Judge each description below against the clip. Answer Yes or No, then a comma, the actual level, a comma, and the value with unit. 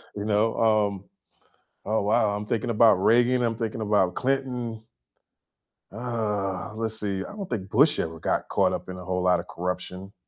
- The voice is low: Yes, low, 105 Hz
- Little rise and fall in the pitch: No, average, 3.2 semitones